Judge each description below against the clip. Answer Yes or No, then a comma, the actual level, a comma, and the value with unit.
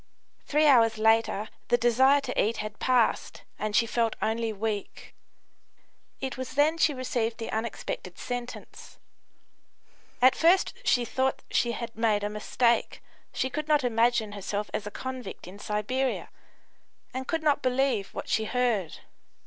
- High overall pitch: Yes, high, 235 Hz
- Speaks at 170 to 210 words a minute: No, average, 150 wpm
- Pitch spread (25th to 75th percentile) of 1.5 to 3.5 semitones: Yes, average, 3.2 semitones